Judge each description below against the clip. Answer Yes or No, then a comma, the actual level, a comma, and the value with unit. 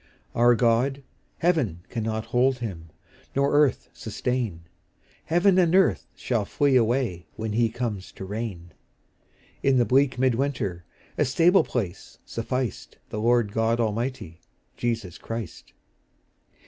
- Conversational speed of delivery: No, slow, 125 wpm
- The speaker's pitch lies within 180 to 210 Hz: No, low, 120 Hz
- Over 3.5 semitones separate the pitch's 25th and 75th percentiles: Yes, average, 3.9 semitones